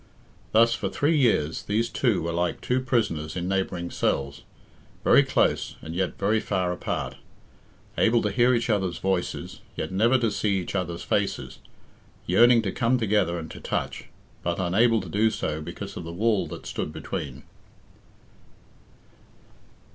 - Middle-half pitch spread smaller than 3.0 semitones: No, average, 4.8 semitones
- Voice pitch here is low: Yes, low, 100 Hz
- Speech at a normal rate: Yes, average, 155 wpm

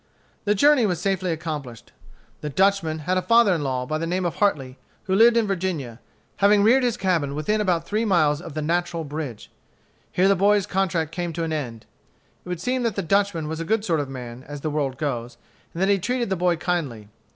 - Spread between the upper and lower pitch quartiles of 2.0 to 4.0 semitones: No, average, 4.9 semitones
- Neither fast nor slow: No, fast, 220 wpm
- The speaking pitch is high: No, medium, 175 Hz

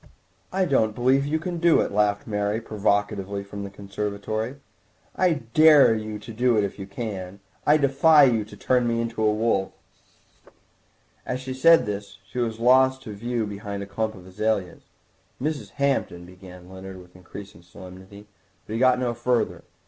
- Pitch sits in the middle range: No, low, 110 Hz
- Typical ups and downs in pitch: Yes, average, 4.2 semitones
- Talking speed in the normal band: Yes, average, 170 wpm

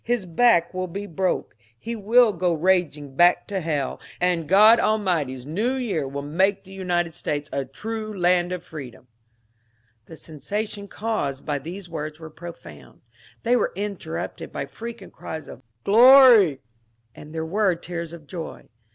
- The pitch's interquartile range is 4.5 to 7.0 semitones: Yes, average, 5.1 semitones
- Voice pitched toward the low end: No, medium, 175 Hz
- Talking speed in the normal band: Yes, average, 160 wpm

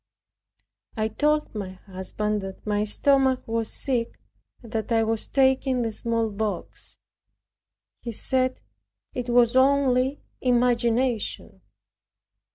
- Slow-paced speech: Yes, slow, 105 wpm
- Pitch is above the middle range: Yes, high, 235 Hz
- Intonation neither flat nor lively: Yes, average, 3.1 semitones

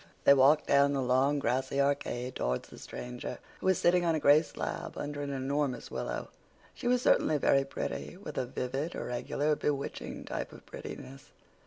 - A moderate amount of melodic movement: No, narrow, 2.2 semitones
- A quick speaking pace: No, average, 175 wpm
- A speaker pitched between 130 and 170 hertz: Yes, medium, 140 Hz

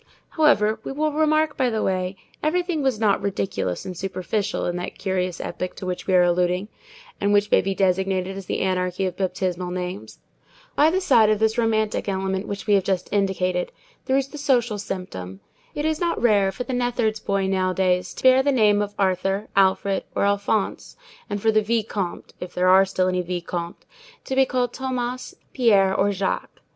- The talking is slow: No, average, 185 wpm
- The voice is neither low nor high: No, high, 200 Hz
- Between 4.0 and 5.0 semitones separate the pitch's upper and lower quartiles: Yes, average, 4.5 semitones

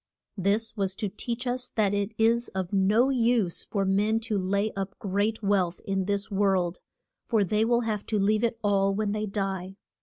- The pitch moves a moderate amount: No, narrow, 2.3 semitones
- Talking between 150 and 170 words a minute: No, average, 190 wpm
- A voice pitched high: Yes, high, 205 Hz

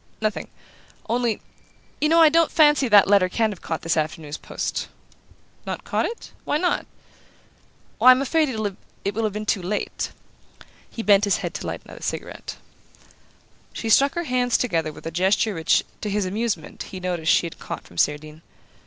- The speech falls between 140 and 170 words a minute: No, average, 180 wpm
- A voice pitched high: Yes, high, 210 Hz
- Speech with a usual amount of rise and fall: No, wide, 6.0 semitones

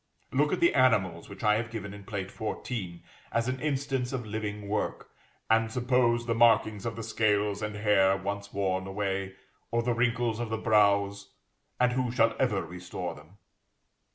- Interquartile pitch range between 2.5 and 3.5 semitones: Yes, average, 2.9 semitones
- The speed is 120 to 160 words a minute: No, average, 175 wpm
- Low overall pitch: Yes, low, 110 Hz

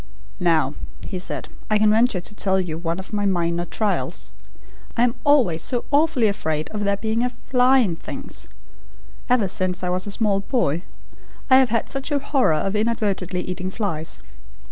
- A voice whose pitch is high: Yes, high, 200 Hz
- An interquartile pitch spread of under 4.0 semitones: No, average, 4.8 semitones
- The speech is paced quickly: No, average, 180 wpm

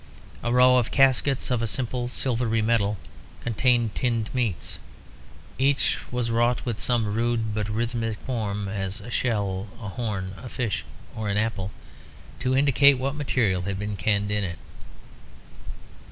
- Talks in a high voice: No, low, 115 Hz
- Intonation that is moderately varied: Yes, average, 3.2 semitones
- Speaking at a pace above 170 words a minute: No, average, 150 wpm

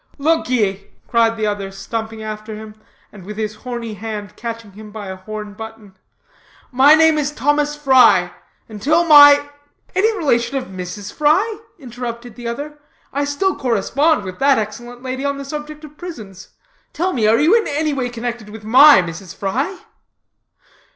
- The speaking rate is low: No, average, 165 wpm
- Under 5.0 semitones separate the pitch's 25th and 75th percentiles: No, wide, 5.5 semitones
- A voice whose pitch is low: No, high, 240 Hz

